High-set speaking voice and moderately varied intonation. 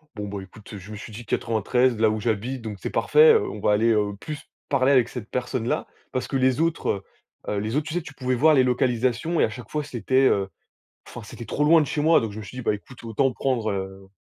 No: low, 120 Hz; average, 4.0 semitones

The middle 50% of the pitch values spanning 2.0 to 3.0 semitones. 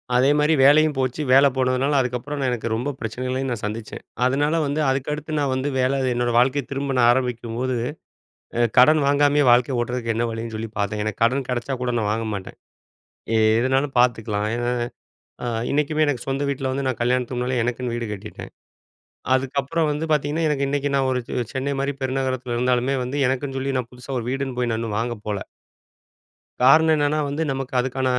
Yes: narrow, 2.6 semitones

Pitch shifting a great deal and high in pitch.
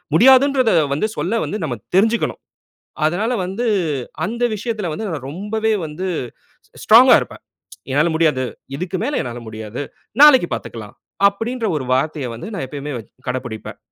No: wide, 8.9 semitones; medium, 180 Hz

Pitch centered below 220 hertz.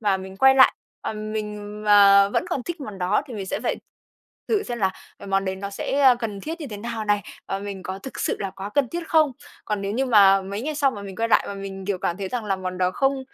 Yes: high, 205 Hz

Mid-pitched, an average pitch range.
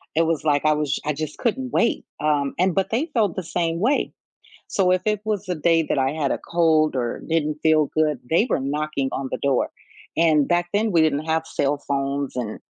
Yes: medium, 155 Hz; average, 3.7 semitones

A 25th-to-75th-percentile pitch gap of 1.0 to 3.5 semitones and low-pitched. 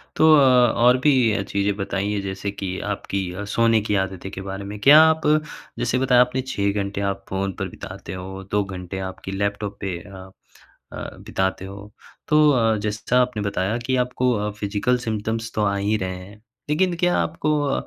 No: average, 4.2 semitones; low, 105 Hz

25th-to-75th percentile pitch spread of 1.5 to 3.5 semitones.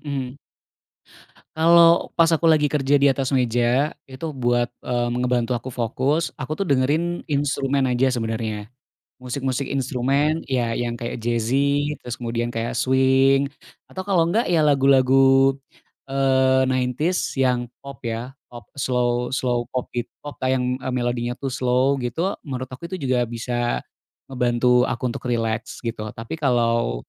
Yes: narrow, 2.4 semitones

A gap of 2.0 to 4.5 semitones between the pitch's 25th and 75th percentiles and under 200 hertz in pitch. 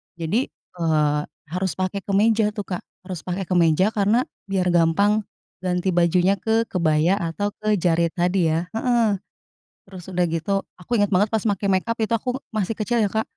Yes: average, 3.4 semitones; high, 190 Hz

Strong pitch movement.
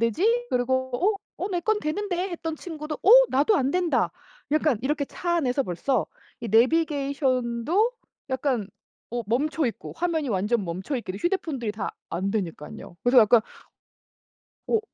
Yes: wide, 6.1 semitones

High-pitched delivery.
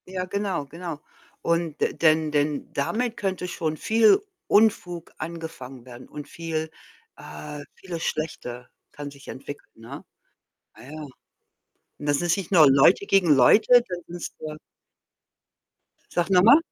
No: medium, 165 Hz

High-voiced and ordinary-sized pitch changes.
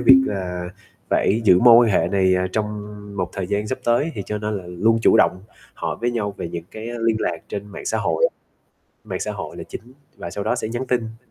No: low, 105 Hz; average, 3.8 semitones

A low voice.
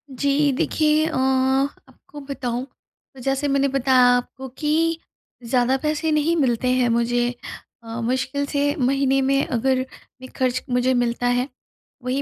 No: very high, 265 Hz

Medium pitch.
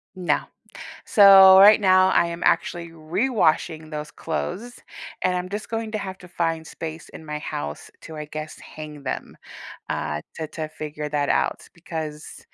Yes: medium, 165 Hz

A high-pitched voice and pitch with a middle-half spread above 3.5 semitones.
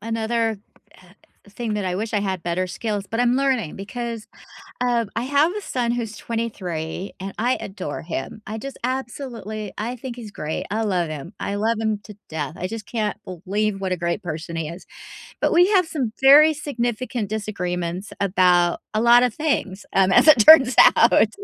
Yes: high, 215 Hz; average, 4.6 semitones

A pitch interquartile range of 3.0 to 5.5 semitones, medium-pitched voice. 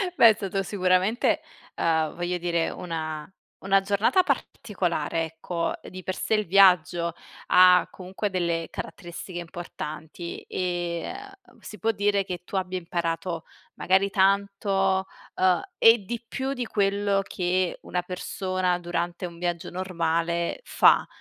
No: narrow, 2.5 semitones; medium, 180 Hz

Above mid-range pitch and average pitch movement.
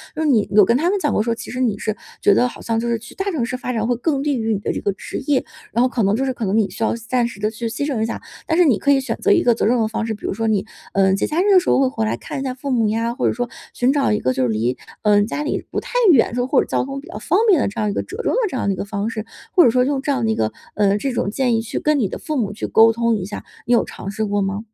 Yes: high, 230 Hz; average, 4.3 semitones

